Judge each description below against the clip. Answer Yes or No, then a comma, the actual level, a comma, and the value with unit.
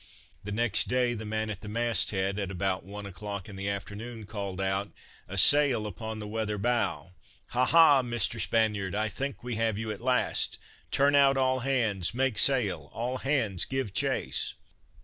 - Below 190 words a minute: Yes, average, 180 wpm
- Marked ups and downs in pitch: No, average, 3.6 semitones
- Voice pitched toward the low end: Yes, low, 110 Hz